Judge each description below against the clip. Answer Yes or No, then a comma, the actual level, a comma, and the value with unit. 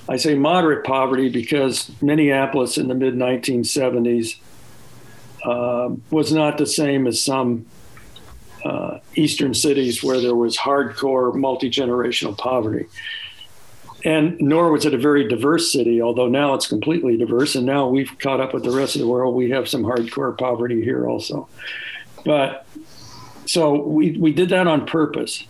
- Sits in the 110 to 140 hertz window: Yes, low, 135 Hz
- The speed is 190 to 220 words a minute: No, average, 155 wpm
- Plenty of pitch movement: No, average, 3.3 semitones